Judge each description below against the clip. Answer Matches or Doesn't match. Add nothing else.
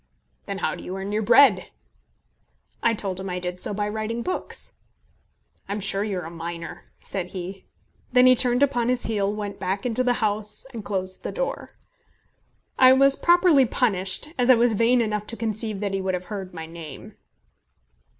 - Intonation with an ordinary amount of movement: Matches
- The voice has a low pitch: Doesn't match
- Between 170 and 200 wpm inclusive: Matches